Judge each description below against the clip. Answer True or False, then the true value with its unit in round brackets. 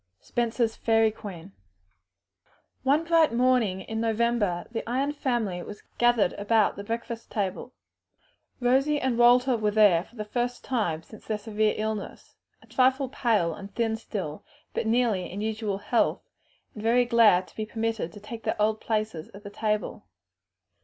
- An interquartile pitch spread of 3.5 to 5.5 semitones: False (2.6 semitones)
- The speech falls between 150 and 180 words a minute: True (160 wpm)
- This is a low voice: False (220 Hz)